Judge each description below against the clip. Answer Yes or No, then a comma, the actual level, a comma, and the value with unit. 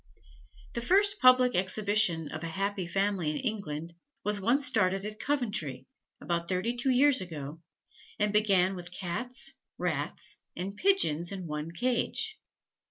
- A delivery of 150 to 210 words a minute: No, average, 140 wpm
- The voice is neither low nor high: No, high, 200 Hz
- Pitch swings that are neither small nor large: No, wide, 6.0 semitones